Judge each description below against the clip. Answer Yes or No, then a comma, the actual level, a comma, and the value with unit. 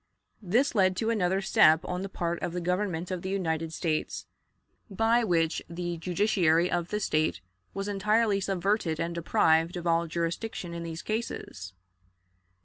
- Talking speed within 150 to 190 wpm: Yes, average, 155 wpm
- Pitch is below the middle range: No, medium, 180 Hz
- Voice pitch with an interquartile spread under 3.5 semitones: Yes, average, 2.9 semitones